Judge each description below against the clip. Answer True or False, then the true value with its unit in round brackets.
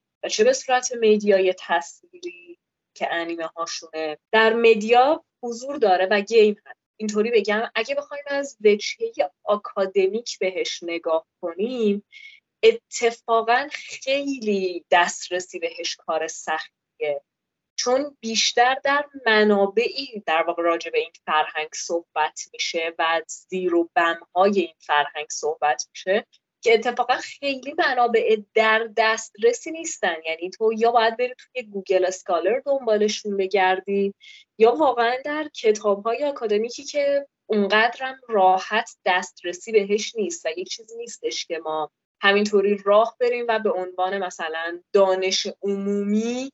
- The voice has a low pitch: False (215 Hz)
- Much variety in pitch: True (5.9 semitones)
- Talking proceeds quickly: False (125 wpm)